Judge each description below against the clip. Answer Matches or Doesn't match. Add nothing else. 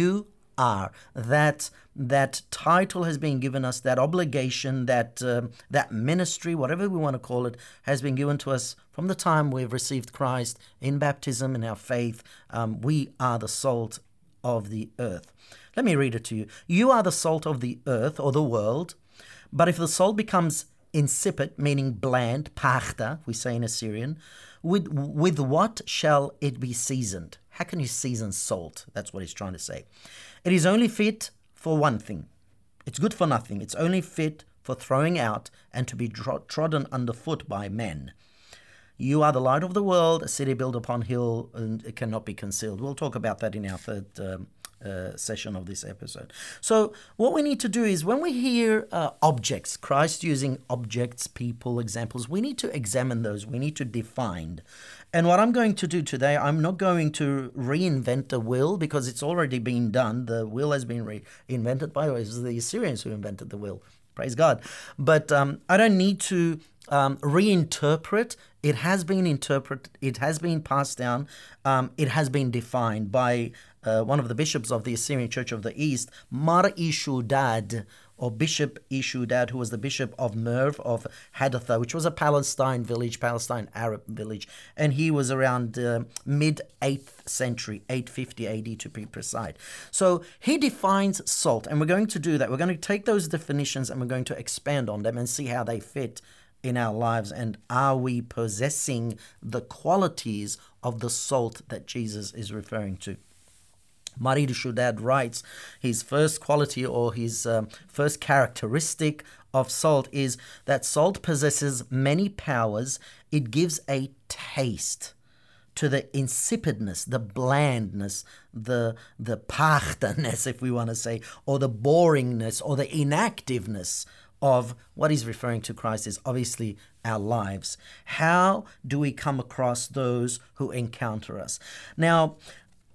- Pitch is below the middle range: Matches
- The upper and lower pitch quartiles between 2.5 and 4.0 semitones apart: Doesn't match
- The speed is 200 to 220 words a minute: Doesn't match